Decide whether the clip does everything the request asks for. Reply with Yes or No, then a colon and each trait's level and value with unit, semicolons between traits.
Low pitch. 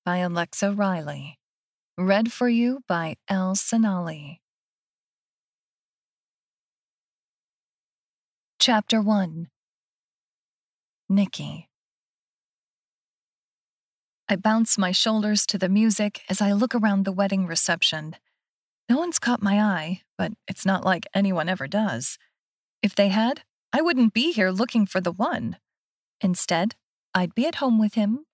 No: high, 200 Hz